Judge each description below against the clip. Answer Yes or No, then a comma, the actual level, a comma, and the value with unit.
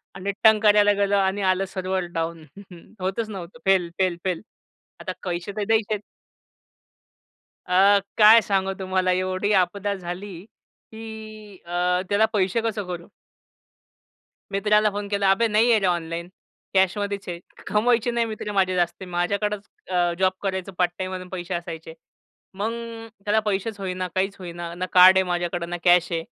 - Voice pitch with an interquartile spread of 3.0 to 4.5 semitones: No, narrow, 2.5 semitones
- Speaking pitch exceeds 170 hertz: Yes, high, 190 Hz